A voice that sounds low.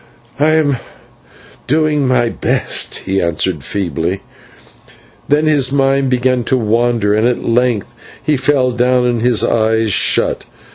Yes: low, 125 Hz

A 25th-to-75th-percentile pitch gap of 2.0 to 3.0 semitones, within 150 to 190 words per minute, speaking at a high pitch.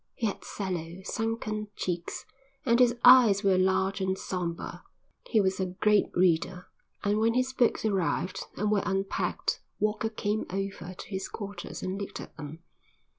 Yes: narrow, 2.5 semitones; average, 160 wpm; high, 195 Hz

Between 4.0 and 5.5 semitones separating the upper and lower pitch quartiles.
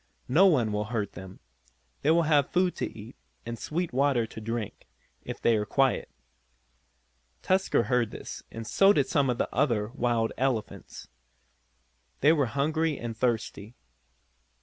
Yes: average, 4.8 semitones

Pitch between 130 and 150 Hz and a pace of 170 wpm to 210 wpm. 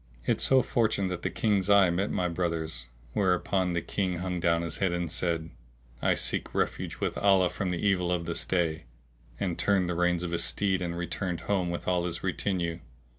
No: very low, 90 Hz; average, 200 wpm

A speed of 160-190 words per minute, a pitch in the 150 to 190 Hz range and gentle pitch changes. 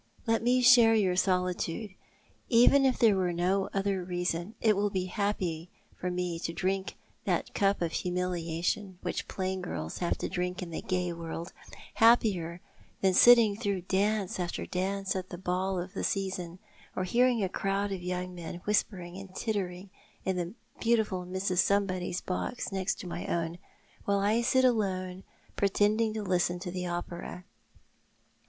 Yes: average, 170 wpm; medium, 185 Hz; narrow, 2.3 semitones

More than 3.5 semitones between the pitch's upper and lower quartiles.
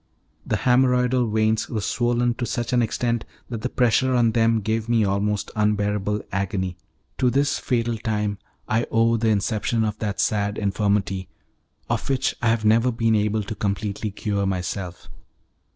No: narrow, 2.5 semitones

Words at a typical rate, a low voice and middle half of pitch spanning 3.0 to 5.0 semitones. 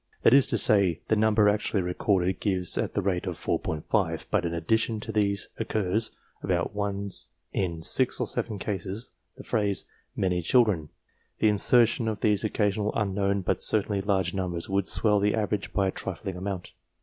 No: average, 175 wpm; low, 100 Hz; narrow, 2.5 semitones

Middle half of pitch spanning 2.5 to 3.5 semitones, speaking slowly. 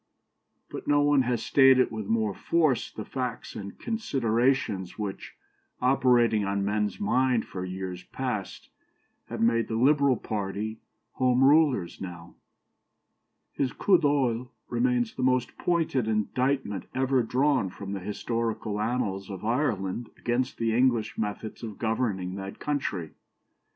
No: average, 4.4 semitones; slow, 130 wpm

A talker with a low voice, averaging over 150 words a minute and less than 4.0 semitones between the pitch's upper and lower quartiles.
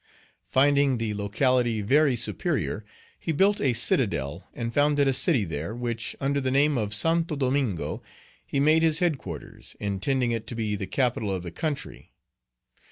No: low, 125 Hz; average, 160 wpm; average, 5.2 semitones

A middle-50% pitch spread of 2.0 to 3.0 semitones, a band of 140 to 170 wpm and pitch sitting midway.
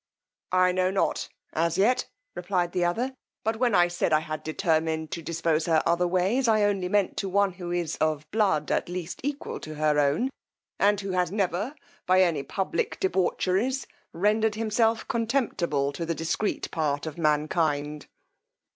No: average, 4.6 semitones; average, 165 wpm; medium, 180 Hz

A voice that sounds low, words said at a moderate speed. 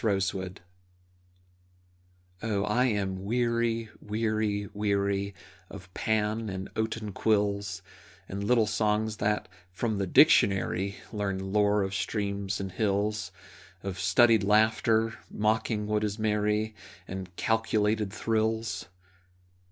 No: low, 105 Hz; slow, 105 wpm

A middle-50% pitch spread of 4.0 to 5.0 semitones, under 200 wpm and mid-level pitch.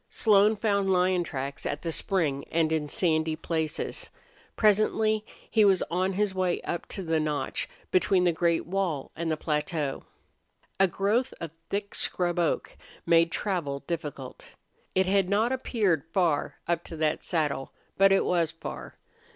No: average, 3.6 semitones; average, 155 wpm; medium, 175 Hz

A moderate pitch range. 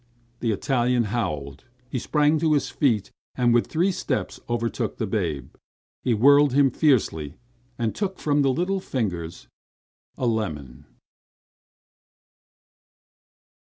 No: wide, 5.7 semitones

